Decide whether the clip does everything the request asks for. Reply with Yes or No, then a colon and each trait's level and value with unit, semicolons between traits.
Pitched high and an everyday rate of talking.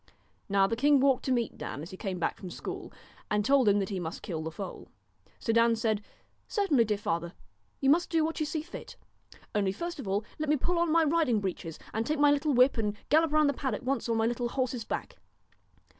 No: high, 240 Hz; fast, 235 wpm